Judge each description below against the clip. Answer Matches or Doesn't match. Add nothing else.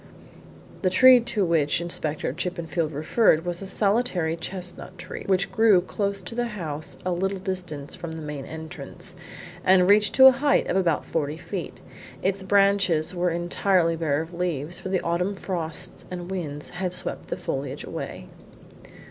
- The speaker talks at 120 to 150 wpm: Doesn't match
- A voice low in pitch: Doesn't match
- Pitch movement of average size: Matches